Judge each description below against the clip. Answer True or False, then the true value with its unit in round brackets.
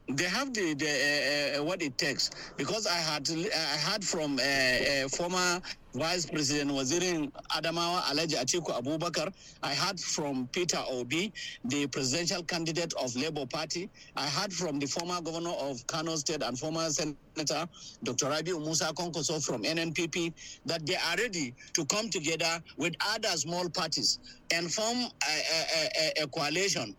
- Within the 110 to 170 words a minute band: True (160 wpm)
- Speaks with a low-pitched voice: False (165 Hz)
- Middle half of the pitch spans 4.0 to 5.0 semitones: False (2.8 semitones)